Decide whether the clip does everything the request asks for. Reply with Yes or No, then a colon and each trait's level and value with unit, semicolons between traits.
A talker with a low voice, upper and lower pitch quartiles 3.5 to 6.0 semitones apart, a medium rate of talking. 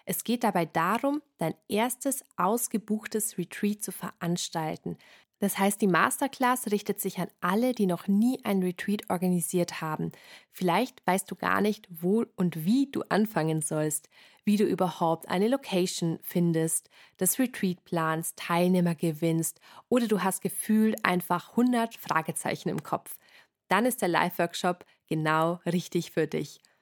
No: medium, 185 Hz; average, 4.0 semitones; average, 145 wpm